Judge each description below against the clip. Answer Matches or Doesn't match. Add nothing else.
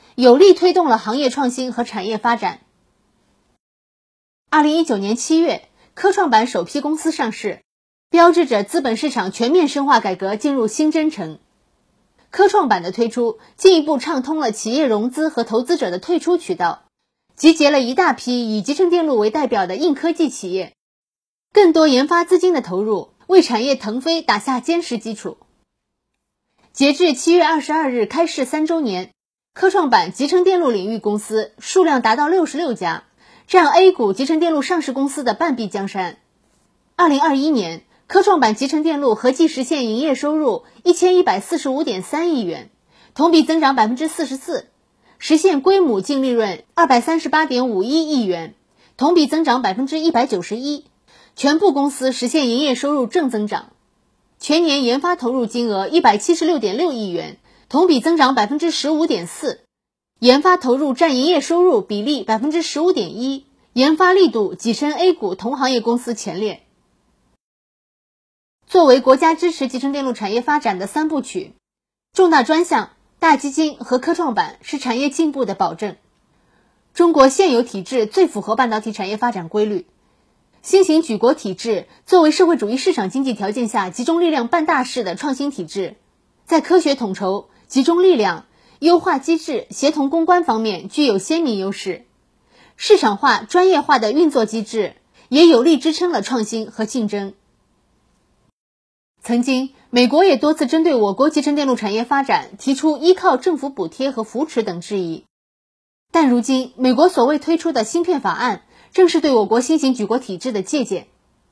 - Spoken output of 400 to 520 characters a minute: Doesn't match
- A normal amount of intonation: Doesn't match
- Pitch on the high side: Matches